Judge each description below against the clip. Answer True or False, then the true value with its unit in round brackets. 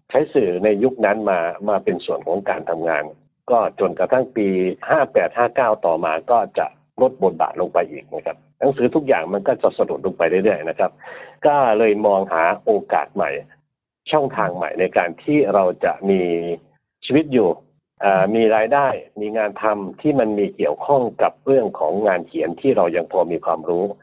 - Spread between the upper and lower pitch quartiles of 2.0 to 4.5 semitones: False (5.1 semitones)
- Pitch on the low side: True (105 Hz)